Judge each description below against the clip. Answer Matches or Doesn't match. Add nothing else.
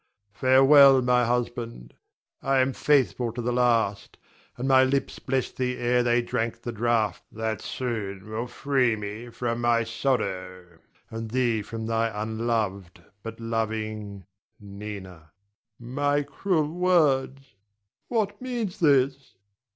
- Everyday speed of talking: Doesn't match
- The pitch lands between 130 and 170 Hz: Doesn't match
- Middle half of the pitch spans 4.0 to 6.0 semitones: Doesn't match